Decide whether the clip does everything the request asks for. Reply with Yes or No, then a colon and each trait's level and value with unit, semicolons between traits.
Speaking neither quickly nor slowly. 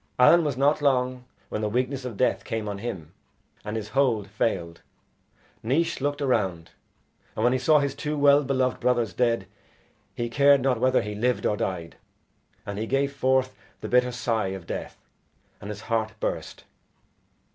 Yes: average, 170 wpm